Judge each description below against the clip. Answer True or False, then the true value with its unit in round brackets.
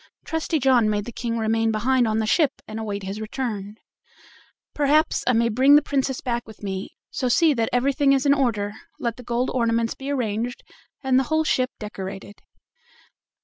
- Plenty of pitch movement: False (3.7 semitones)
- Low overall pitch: False (240 Hz)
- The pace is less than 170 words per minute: False (190 wpm)